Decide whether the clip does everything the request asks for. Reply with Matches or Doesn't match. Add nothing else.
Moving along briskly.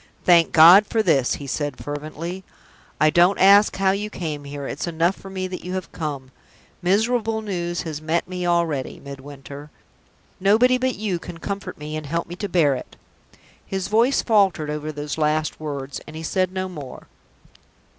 Doesn't match